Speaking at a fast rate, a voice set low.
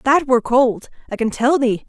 No: fast, 225 wpm; very high, 250 Hz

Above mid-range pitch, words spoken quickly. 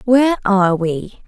No: high, 210 Hz; average, 140 wpm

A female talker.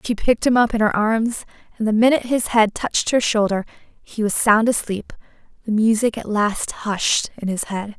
Yes: female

